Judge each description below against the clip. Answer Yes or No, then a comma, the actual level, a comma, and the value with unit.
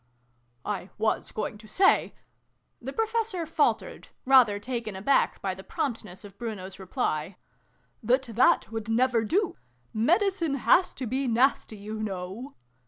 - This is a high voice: Yes, high, 225 Hz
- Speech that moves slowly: No, average, 150 wpm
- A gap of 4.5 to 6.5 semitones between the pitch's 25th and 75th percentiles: Yes, average, 5.0 semitones